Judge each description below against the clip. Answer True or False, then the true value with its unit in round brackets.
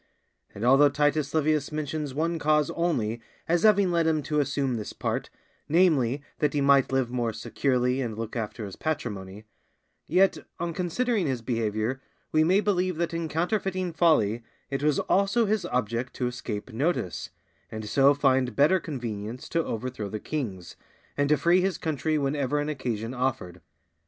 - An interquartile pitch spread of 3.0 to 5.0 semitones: False (5.5 semitones)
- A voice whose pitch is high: False (140 Hz)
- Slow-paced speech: False (165 wpm)